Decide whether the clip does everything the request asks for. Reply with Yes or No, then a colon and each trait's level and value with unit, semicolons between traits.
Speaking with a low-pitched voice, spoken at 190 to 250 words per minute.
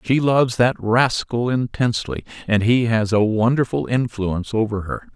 No: low, 115 Hz; average, 150 wpm